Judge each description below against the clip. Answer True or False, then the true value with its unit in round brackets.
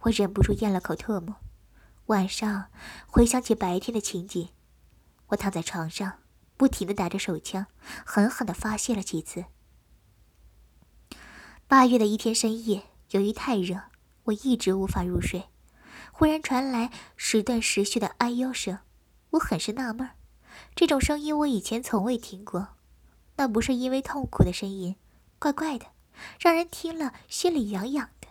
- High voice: True (220 Hz)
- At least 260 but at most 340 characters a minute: False (225 characters per minute)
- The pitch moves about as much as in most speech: True (4.7 semitones)